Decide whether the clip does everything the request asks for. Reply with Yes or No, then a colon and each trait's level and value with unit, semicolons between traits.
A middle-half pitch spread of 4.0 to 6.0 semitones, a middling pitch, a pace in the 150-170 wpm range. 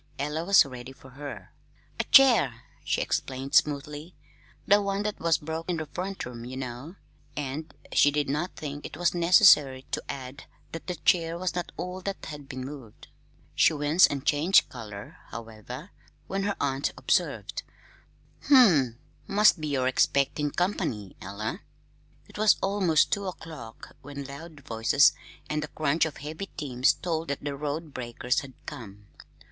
Yes: average, 4.6 semitones; medium, 145 Hz; average, 160 wpm